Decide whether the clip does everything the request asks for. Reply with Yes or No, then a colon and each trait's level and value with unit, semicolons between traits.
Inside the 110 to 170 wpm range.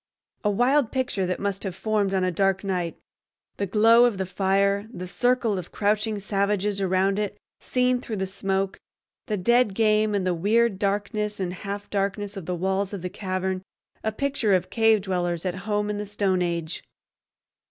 No: average, 180 wpm